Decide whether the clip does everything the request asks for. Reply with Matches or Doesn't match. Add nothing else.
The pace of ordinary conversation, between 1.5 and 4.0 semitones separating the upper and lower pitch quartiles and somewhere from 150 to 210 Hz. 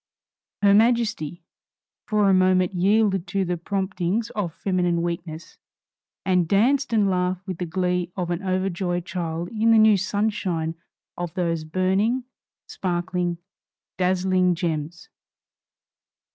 Doesn't match